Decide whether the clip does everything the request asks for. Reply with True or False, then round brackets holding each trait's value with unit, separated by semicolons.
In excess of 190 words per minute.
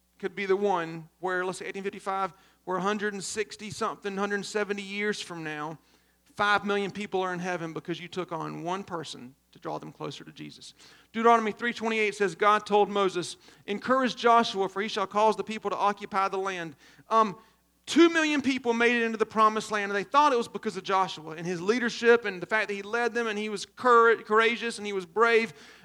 True (200 wpm)